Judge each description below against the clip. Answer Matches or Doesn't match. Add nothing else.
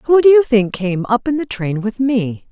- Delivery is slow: Doesn't match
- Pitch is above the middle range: Matches